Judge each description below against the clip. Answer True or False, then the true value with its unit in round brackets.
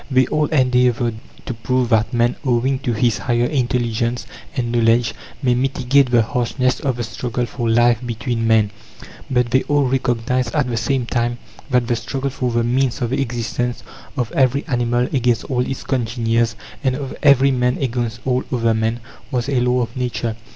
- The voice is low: True (125 Hz)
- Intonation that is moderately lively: False (1.8 semitones)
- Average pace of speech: True (180 wpm)